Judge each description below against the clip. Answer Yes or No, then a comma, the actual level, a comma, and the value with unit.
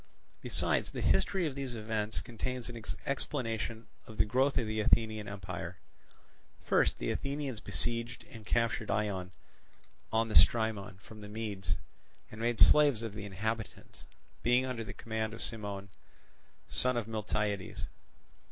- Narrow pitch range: Yes, narrow, 2.3 semitones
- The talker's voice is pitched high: No, low, 110 Hz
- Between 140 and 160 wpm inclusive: Yes, average, 145 wpm